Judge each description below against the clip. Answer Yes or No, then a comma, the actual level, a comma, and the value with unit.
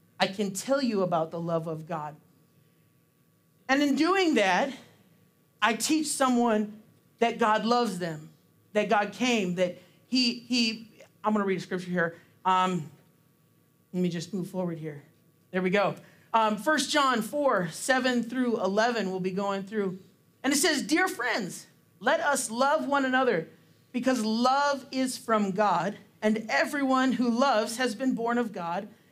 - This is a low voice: No, high, 215 Hz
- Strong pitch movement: Yes, wide, 6.0 semitones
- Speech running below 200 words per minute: Yes, average, 160 wpm